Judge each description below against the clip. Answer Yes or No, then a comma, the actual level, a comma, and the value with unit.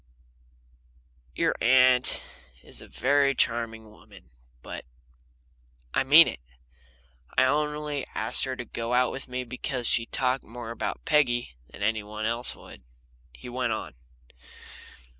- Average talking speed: No, slow, 125 wpm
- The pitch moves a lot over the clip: No, average, 2.7 semitones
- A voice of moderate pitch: No, low, 125 Hz